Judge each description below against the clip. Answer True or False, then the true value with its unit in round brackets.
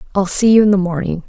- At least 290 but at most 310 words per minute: False (280 wpm)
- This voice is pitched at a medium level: False (195 Hz)